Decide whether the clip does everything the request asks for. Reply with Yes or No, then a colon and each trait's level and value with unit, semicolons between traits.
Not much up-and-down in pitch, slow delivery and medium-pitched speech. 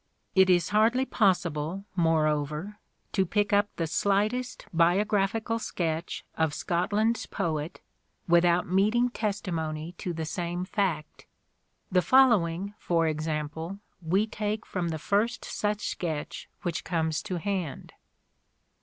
No: average, 4.3 semitones; slow, 120 wpm; medium, 180 Hz